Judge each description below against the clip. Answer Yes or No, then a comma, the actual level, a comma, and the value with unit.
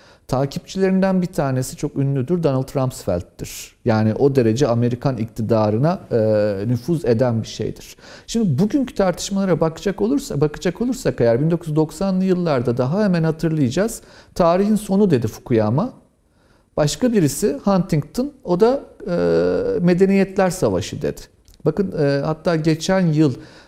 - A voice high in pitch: No, medium, 155 Hz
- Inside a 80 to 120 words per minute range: Yes, average, 115 wpm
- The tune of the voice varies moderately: No, wide, 7.2 semitones